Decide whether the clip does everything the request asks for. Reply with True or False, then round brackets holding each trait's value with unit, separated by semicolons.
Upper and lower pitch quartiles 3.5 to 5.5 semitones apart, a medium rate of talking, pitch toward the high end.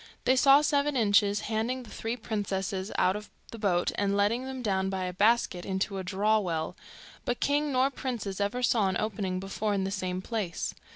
True (4.0 semitones; 195 wpm; 205 Hz)